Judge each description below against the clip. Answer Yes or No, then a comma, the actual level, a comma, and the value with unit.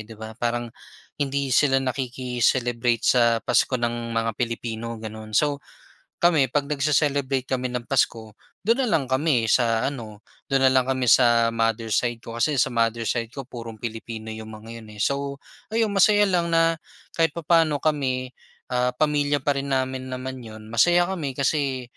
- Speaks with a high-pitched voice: No, low, 130 Hz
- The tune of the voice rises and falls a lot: No, average, 3.5 semitones